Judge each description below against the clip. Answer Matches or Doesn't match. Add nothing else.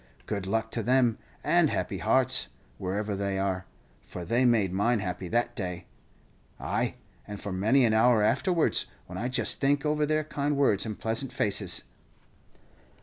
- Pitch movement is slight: Doesn't match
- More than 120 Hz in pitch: Doesn't match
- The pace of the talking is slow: Doesn't match